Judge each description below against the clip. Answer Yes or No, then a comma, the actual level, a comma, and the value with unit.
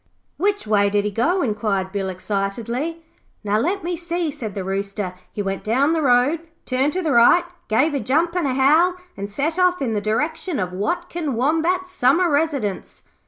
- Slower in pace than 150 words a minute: No, average, 185 wpm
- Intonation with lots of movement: Yes, wide, 8.2 semitones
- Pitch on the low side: No, very high, 265 Hz